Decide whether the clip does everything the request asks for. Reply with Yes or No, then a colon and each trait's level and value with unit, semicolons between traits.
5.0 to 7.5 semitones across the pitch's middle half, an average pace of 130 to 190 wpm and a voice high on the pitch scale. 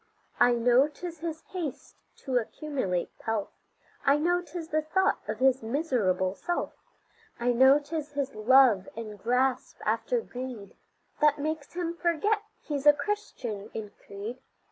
Yes: wide, 5.5 semitones; average, 145 wpm; very high, 270 Hz